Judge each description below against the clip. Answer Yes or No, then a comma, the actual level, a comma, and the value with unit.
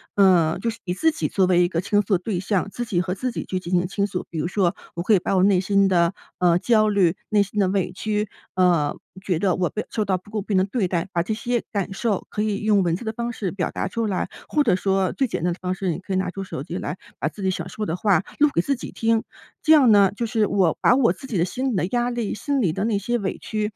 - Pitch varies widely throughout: No, average, 3.2 semitones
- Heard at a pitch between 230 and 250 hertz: No, high, 195 Hz